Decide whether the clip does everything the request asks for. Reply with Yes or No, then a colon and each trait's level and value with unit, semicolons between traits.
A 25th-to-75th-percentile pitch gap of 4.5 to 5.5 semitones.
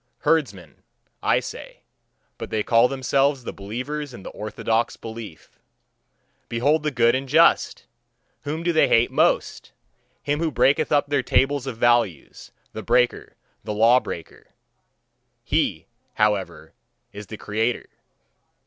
Yes: average, 4.9 semitones